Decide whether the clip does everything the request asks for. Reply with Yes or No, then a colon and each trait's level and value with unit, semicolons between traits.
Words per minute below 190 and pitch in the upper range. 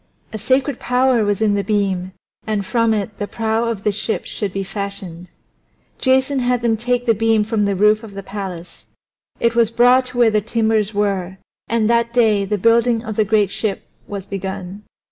No: average, 195 wpm; high, 215 Hz